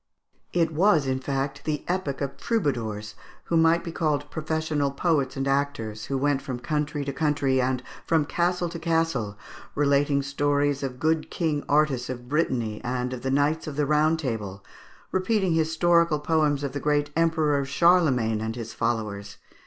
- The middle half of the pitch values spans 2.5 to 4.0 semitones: Yes, average, 3.5 semitones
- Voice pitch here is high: No, medium, 145 Hz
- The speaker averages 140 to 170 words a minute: Yes, average, 165 wpm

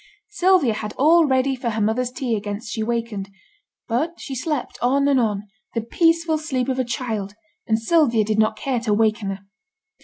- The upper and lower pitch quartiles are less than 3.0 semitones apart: No, average, 4.2 semitones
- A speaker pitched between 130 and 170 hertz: No, high, 235 Hz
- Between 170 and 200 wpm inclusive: Yes, average, 185 wpm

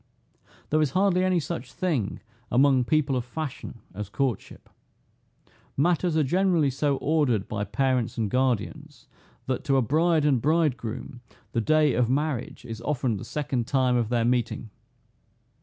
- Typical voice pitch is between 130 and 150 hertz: Yes, low, 135 Hz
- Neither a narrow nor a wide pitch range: Yes, average, 4.4 semitones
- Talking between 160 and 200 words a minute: No, average, 150 wpm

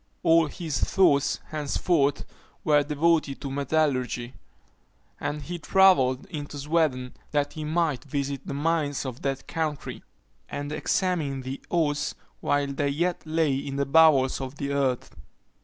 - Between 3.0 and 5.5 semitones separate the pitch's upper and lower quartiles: No, narrow, 2.5 semitones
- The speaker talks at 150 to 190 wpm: No, average, 140 wpm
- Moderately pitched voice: Yes, medium, 145 Hz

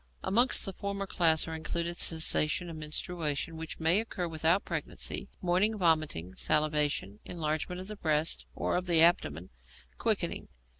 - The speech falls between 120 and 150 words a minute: Yes, average, 145 wpm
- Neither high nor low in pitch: Yes, medium, 165 Hz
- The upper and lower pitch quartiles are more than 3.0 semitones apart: No, average, 2.7 semitones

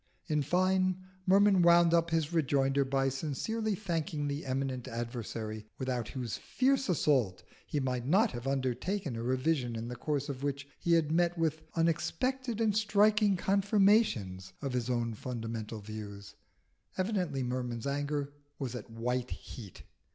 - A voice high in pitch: No, medium, 140 Hz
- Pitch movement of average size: No, wide, 6.4 semitones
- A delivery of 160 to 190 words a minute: No, average, 145 wpm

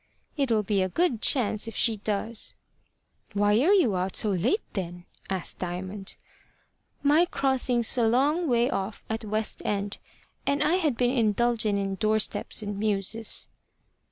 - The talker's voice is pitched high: Yes, high, 220 Hz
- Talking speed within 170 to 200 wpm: No, average, 155 wpm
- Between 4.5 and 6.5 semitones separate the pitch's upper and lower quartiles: No, average, 3.9 semitones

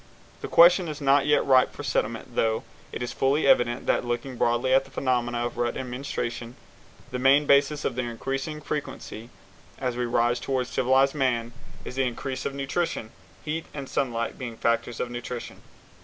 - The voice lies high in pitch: No, low, 125 Hz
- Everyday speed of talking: Yes, average, 175 wpm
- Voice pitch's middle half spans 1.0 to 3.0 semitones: Yes, narrow, 2.6 semitones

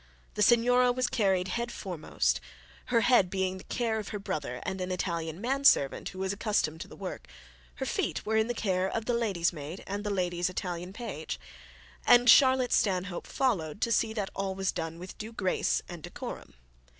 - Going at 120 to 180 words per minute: No, average, 195 wpm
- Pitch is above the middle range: Yes, high, 195 Hz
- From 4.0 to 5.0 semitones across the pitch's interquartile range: Yes, average, 4.3 semitones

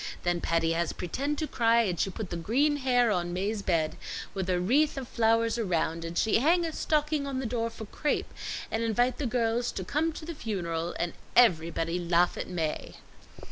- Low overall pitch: No, high, 220 Hz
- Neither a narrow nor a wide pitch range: No, wide, 6.6 semitones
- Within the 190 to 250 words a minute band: Yes, average, 200 wpm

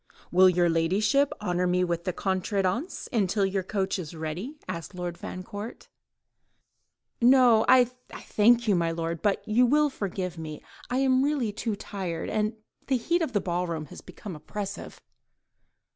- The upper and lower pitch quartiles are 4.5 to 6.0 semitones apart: Yes, average, 5.1 semitones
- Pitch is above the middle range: Yes, high, 195 Hz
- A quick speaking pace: No, average, 155 wpm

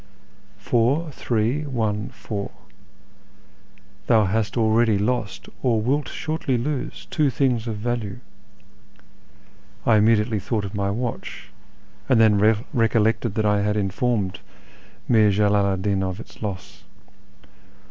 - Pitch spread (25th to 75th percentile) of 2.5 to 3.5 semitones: Yes, average, 2.8 semitones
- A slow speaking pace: Yes, slow, 125 wpm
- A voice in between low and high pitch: No, low, 110 Hz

